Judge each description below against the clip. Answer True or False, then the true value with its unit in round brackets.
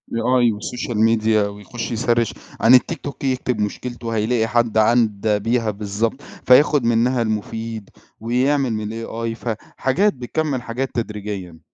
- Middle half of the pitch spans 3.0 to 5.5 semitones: False (2.5 semitones)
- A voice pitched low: True (115 Hz)